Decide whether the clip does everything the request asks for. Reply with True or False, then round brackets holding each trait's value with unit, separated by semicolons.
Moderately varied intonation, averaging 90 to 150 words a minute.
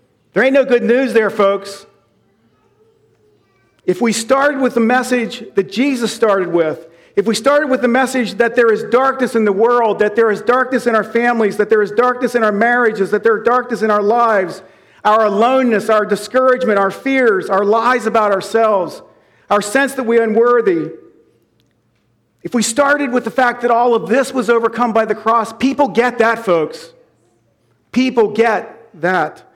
False (3.1 semitones; 180 wpm)